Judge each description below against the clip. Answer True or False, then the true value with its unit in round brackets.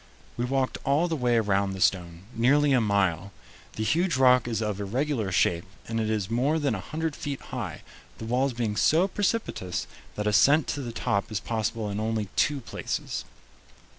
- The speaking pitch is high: False (115 Hz)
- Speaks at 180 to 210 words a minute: True (185 wpm)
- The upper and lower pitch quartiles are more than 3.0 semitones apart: True (5.2 semitones)